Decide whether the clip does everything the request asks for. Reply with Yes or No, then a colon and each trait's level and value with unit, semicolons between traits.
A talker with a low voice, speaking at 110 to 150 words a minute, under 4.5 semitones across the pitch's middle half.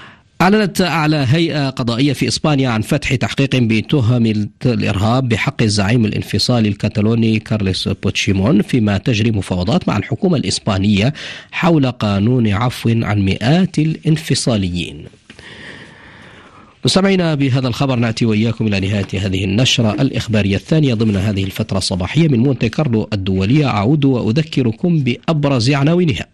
No: low, 120 Hz; average, 120 wpm; average, 5.2 semitones